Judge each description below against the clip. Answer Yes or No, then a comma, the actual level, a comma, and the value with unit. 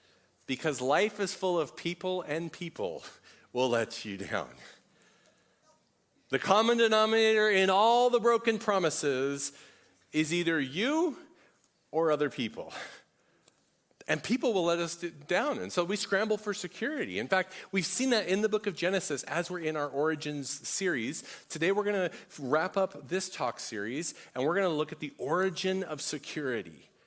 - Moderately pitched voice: Yes, medium, 180 Hz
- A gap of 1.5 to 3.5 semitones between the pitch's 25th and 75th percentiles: No, average, 5.0 semitones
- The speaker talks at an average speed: Yes, average, 160 wpm